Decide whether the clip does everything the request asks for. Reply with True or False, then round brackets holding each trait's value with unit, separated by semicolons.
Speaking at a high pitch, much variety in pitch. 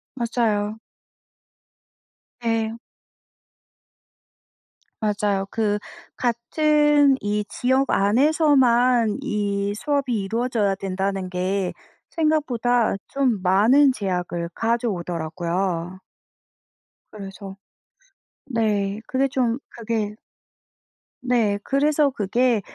False (225 Hz; 4.4 semitones)